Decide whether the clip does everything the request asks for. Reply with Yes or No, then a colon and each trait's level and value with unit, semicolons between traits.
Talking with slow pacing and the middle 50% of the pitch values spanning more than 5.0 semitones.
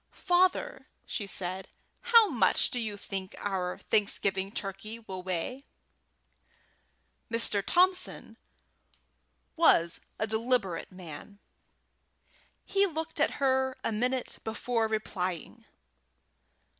Yes: slow, 95 wpm; wide, 5.6 semitones